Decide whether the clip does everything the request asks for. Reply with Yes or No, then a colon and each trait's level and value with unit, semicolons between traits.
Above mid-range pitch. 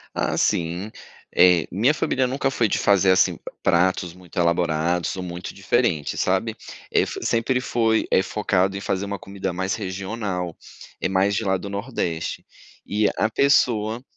No: very low, 95 Hz